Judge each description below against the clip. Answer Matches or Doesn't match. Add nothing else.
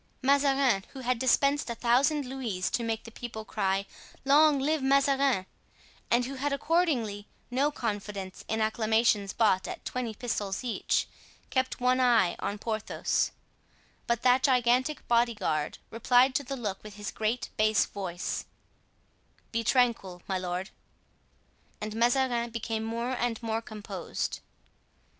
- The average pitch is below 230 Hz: Doesn't match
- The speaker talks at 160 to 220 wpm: Doesn't match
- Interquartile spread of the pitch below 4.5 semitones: Matches